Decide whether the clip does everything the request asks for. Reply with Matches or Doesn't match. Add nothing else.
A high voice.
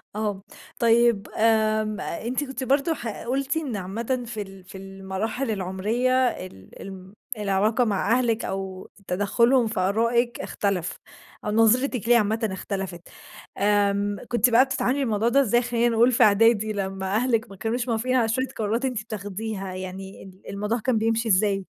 Matches